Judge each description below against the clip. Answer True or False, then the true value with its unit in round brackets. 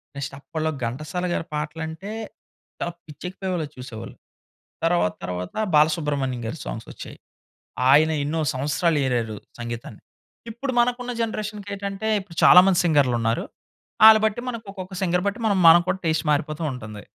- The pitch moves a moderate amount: False (5.9 semitones)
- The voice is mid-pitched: True (160 Hz)